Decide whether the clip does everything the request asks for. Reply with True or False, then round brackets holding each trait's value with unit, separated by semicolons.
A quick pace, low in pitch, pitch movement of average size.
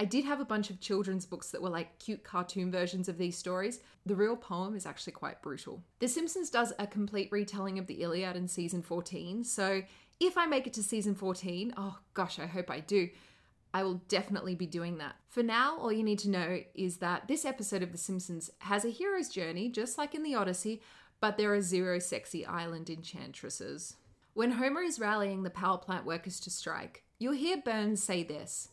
False (210 wpm; 195 Hz; 3.4 semitones)